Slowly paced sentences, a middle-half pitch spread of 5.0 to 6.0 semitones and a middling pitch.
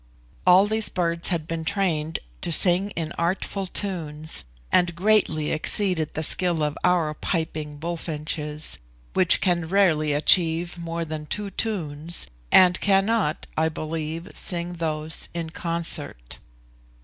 No: slow, 125 wpm; average, 2.7 semitones; medium, 170 Hz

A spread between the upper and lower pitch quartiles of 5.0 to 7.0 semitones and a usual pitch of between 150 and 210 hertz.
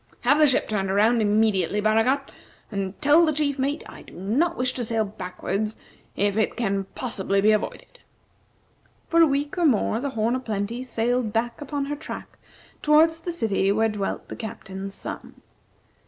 No: wide, 5.5 semitones; high, 225 Hz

